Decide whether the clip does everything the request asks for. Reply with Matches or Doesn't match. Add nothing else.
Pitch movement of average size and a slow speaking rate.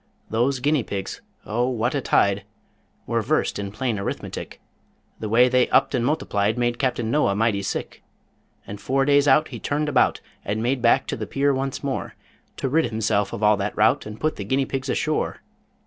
Doesn't match